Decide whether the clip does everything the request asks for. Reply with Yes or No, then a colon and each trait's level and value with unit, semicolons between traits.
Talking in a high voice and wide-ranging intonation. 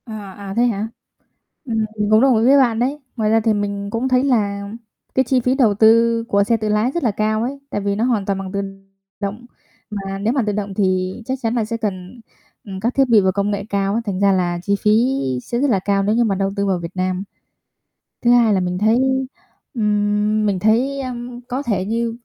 No: high, 215 Hz; average, 3.0 semitones